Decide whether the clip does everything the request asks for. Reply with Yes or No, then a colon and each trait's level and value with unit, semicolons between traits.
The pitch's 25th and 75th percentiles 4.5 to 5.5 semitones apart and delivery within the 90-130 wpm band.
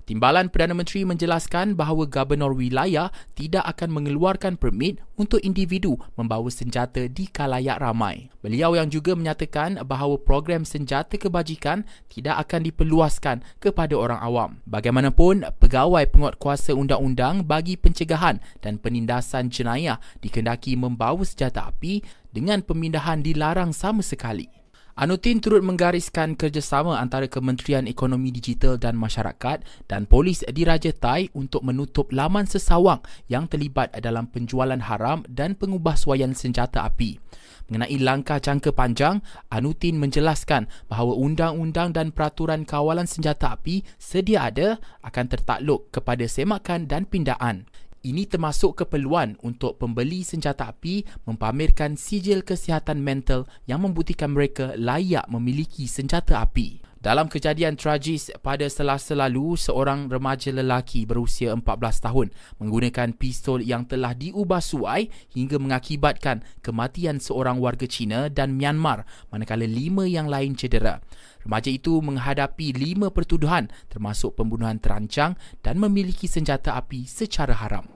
Yes: average, 5.1 semitones; average, 125 wpm